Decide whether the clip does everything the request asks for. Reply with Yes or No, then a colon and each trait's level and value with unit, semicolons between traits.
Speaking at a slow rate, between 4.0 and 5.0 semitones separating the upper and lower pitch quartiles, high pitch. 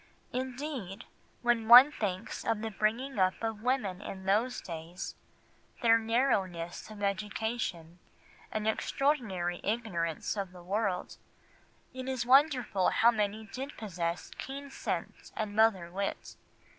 Yes: slow, 125 wpm; average, 4.3 semitones; high, 215 Hz